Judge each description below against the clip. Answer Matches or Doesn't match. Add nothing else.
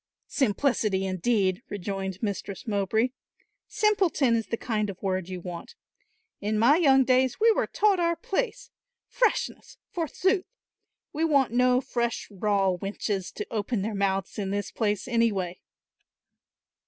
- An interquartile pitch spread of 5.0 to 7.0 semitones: Matches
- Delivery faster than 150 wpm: Doesn't match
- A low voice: Doesn't match